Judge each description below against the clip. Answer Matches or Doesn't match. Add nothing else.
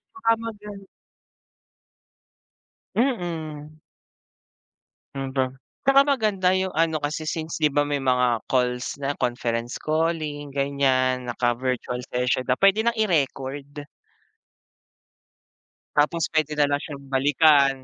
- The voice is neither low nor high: Matches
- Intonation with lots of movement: Doesn't match